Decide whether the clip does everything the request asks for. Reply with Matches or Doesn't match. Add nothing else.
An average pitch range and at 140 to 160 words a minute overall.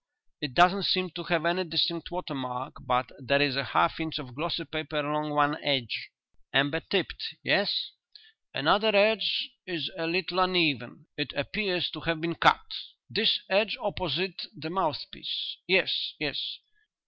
Matches